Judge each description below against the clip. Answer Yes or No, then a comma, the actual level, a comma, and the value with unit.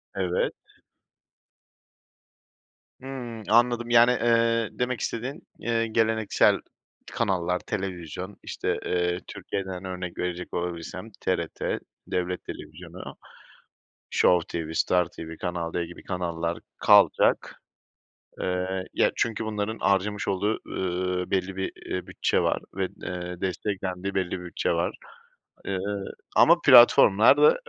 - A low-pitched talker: Yes, very low, 95 Hz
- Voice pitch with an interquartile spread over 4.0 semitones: No, average, 3.7 semitones